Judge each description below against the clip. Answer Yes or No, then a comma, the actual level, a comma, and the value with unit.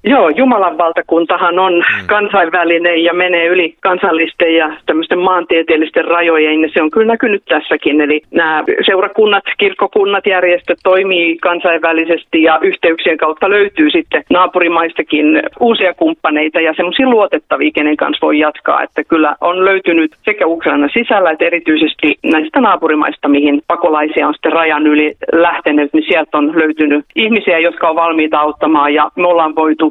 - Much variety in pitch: No, average, 3.1 semitones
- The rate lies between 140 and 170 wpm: Yes, average, 145 wpm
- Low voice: No, medium, 165 Hz